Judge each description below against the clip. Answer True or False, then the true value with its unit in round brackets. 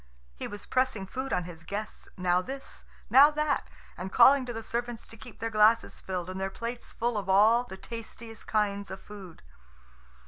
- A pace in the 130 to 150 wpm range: False (185 wpm)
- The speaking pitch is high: True (220 Hz)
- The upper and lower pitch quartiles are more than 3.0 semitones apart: True (3.9 semitones)